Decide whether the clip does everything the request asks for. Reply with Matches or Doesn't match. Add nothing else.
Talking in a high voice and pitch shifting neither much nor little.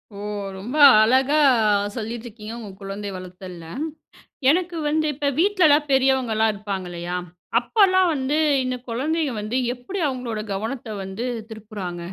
Doesn't match